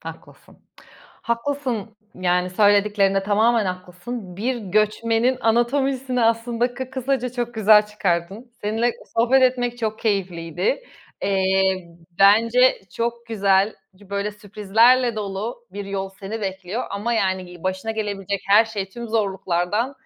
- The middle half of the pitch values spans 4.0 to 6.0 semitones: No, average, 3.5 semitones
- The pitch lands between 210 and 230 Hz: Yes, high, 215 Hz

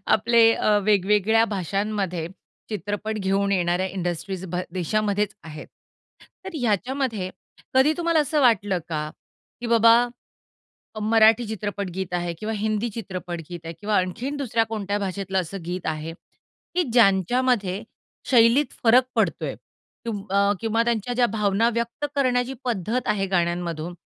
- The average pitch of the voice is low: No, high, 205 Hz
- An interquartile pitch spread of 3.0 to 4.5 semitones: Yes, average, 3.8 semitones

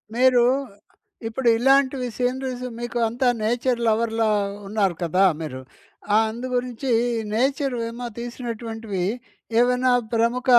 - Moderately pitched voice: No, high, 240 Hz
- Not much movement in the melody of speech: Yes, narrow, 2.1 semitones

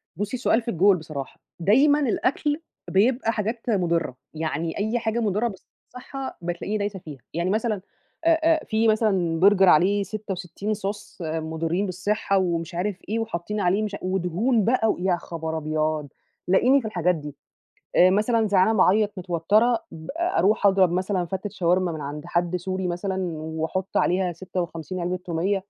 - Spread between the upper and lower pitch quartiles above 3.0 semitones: Yes, average, 3.9 semitones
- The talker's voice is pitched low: No, high, 190 Hz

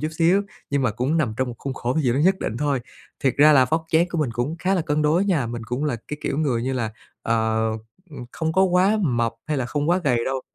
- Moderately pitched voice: Yes, medium, 145 Hz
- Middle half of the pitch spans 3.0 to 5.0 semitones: Yes, average, 4.7 semitones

